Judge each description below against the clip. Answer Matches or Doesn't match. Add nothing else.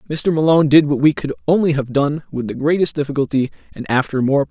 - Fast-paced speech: Matches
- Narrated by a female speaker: Doesn't match